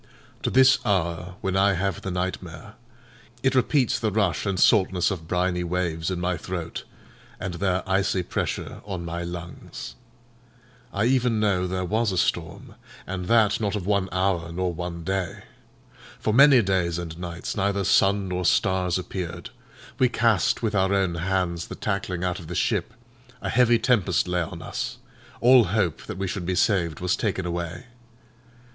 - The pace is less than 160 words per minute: No, average, 170 wpm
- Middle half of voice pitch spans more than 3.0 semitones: No, narrow, 2.6 semitones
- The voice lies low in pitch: Yes, very low, 95 Hz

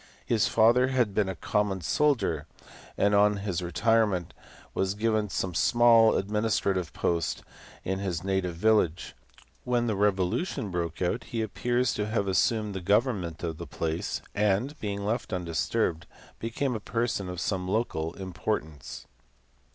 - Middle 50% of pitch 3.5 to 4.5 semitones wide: Yes, average, 4.0 semitones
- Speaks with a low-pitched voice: Yes, low, 100 Hz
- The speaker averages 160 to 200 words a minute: No, average, 145 wpm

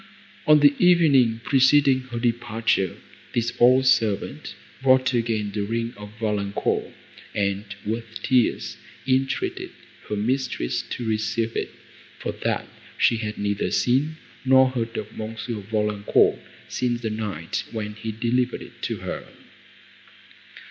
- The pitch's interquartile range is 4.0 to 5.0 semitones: No, average, 3.3 semitones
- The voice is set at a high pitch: No, low, 115 Hz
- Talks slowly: Yes, slow, 130 wpm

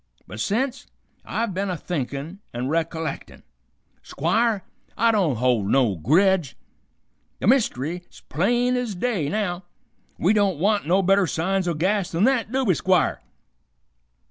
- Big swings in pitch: No, average, 5.0 semitones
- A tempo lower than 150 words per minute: Yes, average, 140 wpm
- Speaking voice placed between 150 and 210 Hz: Yes, medium, 185 Hz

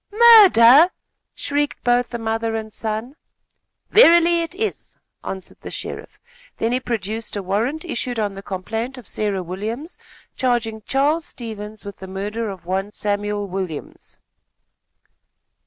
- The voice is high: Yes, high, 225 Hz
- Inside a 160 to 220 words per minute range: No, slow, 135 wpm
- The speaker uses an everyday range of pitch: Yes, average, 4.9 semitones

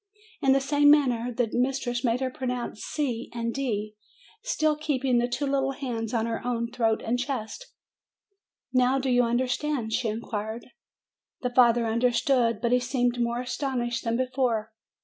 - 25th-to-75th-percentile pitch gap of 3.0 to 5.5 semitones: No, narrow, 2.4 semitones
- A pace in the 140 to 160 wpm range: No, average, 170 wpm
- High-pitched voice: Yes, high, 245 Hz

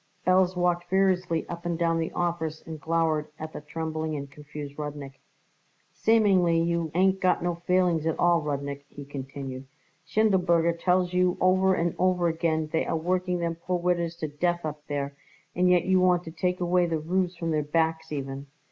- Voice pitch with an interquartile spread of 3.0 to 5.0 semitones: No, narrow, 2.5 semitones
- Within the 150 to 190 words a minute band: Yes, average, 185 wpm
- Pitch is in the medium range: Yes, medium, 170 Hz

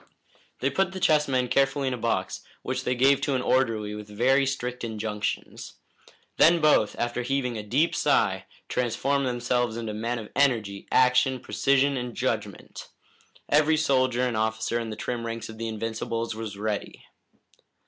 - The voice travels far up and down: No, average, 3.4 semitones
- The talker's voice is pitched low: Yes, low, 125 Hz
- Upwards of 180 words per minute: No, average, 165 wpm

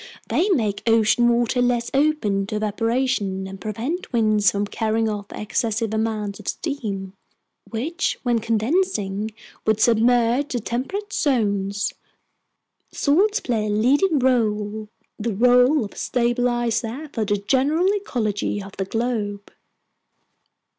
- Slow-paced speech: Yes, slow, 120 wpm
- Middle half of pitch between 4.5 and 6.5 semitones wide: No, average, 3.5 semitones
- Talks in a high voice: Yes, high, 230 Hz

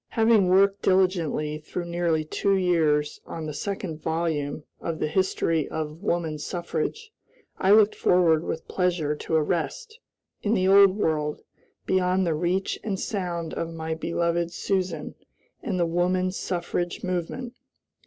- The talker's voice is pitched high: No, medium, 175 Hz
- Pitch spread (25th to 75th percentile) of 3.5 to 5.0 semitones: No, average, 2.9 semitones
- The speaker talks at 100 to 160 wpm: Yes, average, 145 wpm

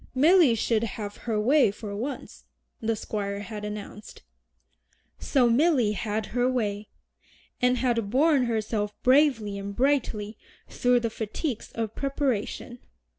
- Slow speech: Yes, slow, 125 wpm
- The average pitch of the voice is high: Yes, high, 230 Hz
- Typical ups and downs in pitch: Yes, average, 3.6 semitones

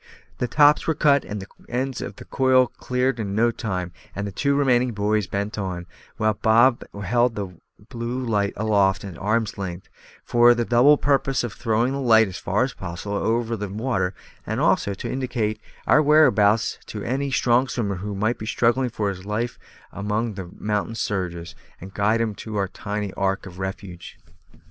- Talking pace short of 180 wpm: No, average, 185 wpm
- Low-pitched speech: Yes, low, 110 Hz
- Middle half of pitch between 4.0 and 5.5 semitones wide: No, average, 3.5 semitones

